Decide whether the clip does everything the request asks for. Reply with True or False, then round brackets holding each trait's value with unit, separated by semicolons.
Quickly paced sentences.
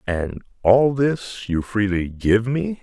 False (150 wpm)